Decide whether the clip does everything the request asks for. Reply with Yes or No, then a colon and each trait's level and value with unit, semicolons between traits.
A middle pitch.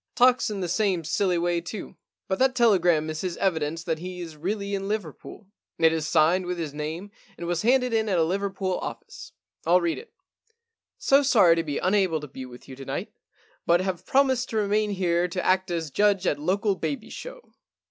Yes: medium, 180 Hz